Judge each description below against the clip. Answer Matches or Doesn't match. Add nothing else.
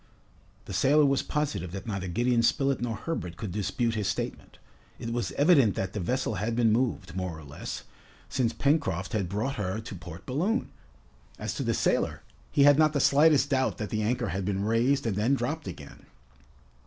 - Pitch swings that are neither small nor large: Doesn't match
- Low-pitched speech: Matches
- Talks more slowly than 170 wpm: Doesn't match